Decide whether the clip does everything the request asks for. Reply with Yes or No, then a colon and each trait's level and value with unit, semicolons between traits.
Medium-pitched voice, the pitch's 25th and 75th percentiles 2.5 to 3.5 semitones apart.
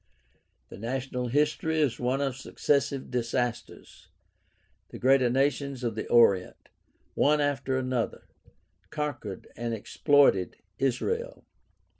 No: low, 130 Hz; average, 2.9 semitones